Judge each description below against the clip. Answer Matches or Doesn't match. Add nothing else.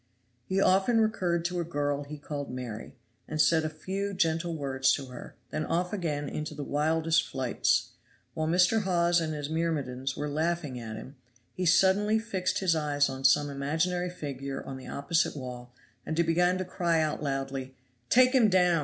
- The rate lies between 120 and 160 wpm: Doesn't match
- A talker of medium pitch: Matches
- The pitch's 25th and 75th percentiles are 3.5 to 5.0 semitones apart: Matches